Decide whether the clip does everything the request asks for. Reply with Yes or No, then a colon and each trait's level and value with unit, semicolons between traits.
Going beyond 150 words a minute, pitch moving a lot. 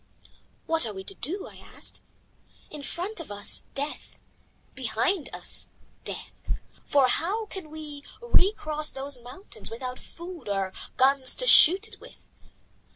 No: average, 140 wpm; wide, 6.5 semitones